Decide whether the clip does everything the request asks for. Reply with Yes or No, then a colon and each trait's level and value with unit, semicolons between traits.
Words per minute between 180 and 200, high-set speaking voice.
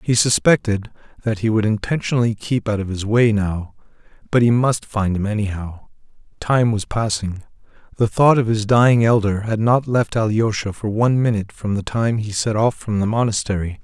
No: average, 185 wpm; low, 110 Hz